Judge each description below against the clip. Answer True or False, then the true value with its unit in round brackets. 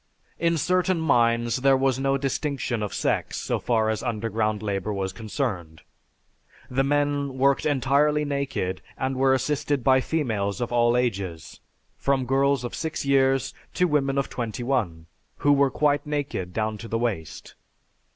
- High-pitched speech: False (130 Hz)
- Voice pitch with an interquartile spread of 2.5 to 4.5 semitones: True (4.2 semitones)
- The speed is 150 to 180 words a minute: True (155 wpm)